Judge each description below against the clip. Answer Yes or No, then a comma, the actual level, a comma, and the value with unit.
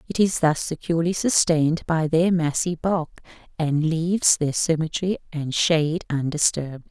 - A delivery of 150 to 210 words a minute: No, average, 140 wpm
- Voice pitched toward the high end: No, medium, 160 Hz